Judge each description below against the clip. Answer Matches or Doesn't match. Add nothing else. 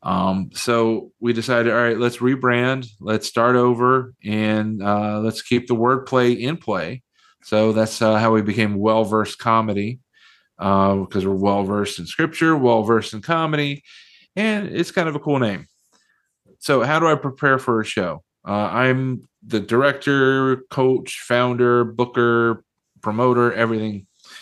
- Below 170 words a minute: Matches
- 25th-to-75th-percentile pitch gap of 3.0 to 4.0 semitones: Matches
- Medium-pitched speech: Doesn't match